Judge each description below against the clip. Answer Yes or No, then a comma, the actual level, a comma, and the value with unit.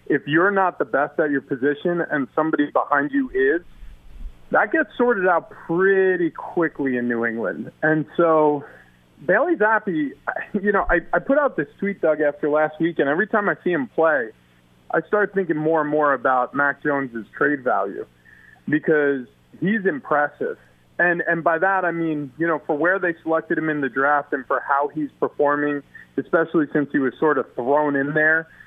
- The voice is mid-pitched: Yes, medium, 150 Hz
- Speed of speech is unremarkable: Yes, average, 185 wpm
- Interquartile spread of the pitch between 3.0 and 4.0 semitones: Yes, average, 3.7 semitones